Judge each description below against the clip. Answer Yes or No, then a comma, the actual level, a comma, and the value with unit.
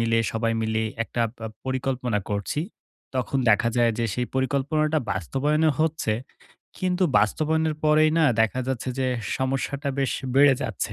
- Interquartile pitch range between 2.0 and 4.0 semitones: No, average, 4.6 semitones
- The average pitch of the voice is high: No, low, 130 Hz